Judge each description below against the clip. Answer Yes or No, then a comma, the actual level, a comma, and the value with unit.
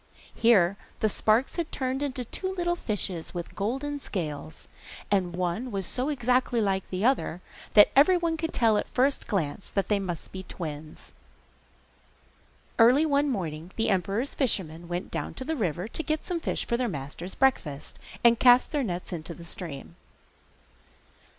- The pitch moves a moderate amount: No, wide, 7.2 semitones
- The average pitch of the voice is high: Yes, high, 215 Hz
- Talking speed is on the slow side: No, average, 165 wpm